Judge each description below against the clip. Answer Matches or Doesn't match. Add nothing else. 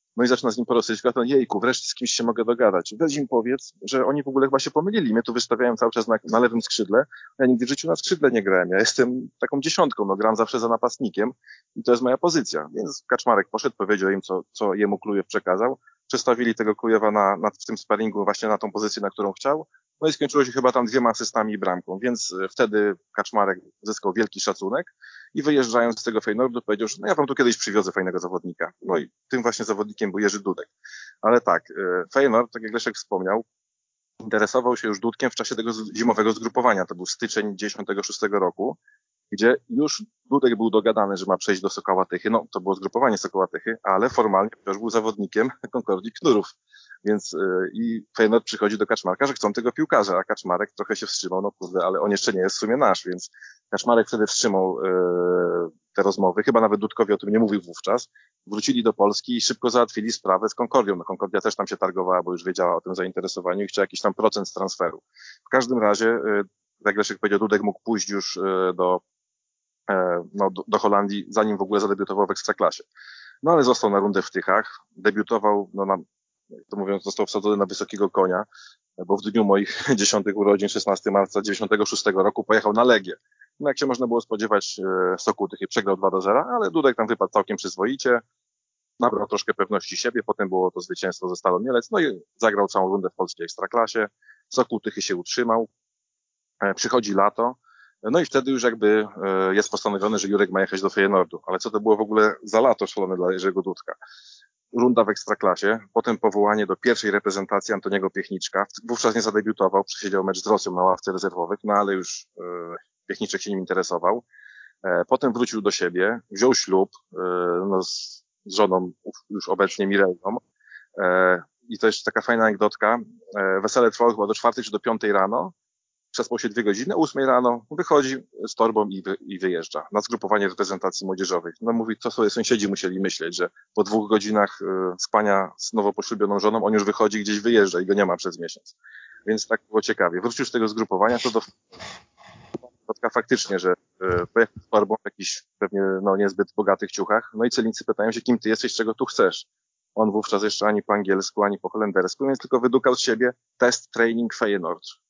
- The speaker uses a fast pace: Matches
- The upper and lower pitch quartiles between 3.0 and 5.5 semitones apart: Matches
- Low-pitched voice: Matches